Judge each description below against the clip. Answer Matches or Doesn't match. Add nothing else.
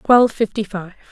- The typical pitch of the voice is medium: Doesn't match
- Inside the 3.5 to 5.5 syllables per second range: Doesn't match